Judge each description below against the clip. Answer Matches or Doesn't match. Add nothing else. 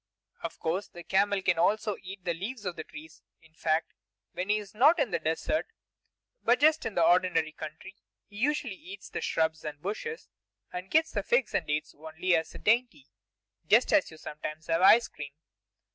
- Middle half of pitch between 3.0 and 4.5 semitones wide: Doesn't match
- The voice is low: Doesn't match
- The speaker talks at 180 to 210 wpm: Matches